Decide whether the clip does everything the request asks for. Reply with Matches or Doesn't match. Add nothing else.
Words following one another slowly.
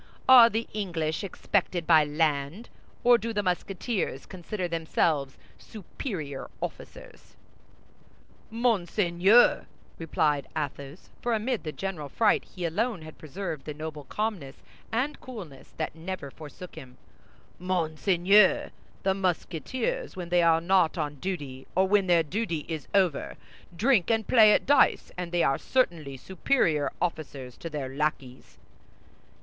Matches